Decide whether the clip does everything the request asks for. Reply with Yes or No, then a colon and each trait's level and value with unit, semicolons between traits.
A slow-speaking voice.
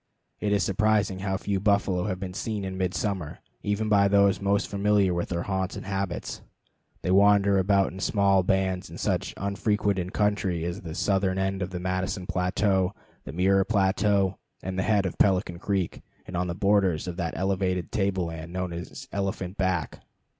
No: average, 180 wpm